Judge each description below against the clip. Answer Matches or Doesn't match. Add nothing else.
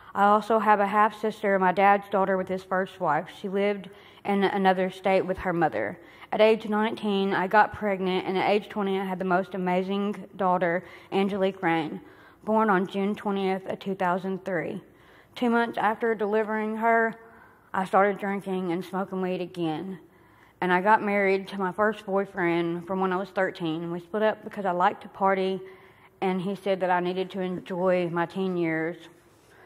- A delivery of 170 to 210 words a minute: Matches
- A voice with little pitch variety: Matches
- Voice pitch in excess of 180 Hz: Matches